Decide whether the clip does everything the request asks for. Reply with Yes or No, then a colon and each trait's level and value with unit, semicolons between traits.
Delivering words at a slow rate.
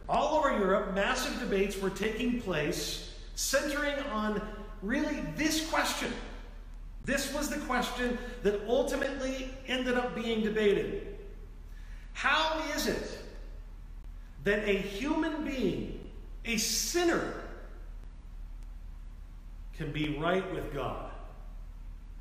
Yes: slow, 100 wpm